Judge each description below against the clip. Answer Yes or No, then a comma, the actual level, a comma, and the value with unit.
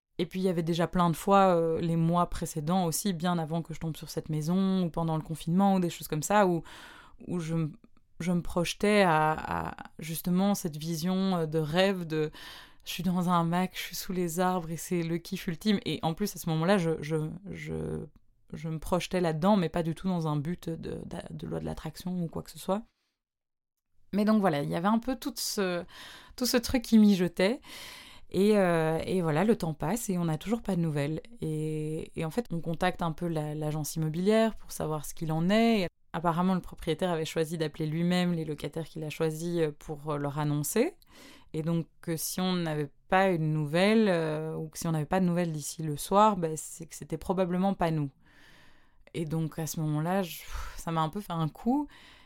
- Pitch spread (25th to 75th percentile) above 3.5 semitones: No, average, 3.0 semitones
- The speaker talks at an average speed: No, fast, 225 wpm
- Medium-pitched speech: Yes, medium, 170 Hz